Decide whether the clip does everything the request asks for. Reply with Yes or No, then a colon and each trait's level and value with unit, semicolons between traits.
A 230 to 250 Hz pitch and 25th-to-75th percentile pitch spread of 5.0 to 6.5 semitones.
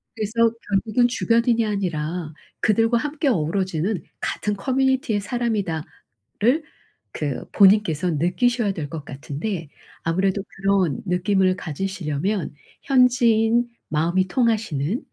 No: high, 200 Hz; wide, 5.6 semitones